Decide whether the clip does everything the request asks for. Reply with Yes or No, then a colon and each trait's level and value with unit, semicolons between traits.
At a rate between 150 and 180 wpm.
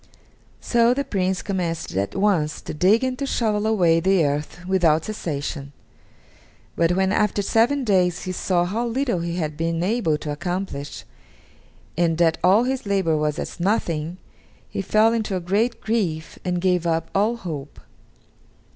Yes: average, 160 wpm